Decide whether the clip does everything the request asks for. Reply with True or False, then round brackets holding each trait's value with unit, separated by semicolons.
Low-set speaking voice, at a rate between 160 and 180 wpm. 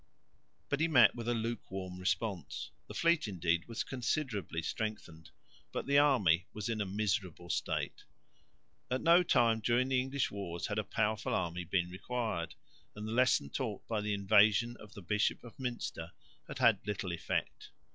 True (105 Hz; 170 wpm)